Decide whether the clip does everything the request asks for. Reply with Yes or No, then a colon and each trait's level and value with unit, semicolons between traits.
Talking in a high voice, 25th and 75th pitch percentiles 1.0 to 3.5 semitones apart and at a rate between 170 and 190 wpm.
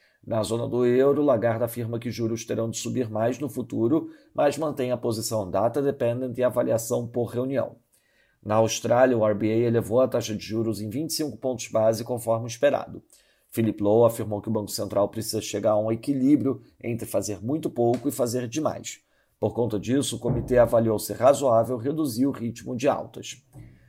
No: low, 120 Hz; narrow, 2.6 semitones; average, 180 wpm